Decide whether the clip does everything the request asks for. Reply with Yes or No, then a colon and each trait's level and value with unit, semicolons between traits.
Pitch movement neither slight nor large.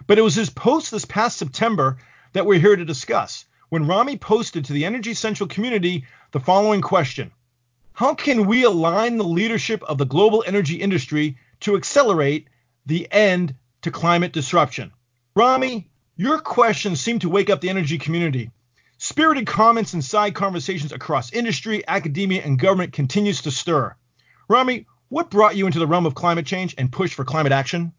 No: wide, 6.2 semitones